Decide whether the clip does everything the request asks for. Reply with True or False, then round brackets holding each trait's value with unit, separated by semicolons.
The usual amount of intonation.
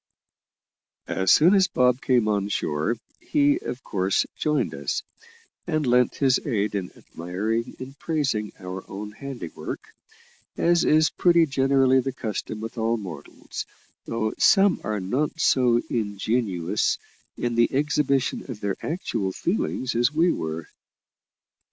False (6.2 semitones)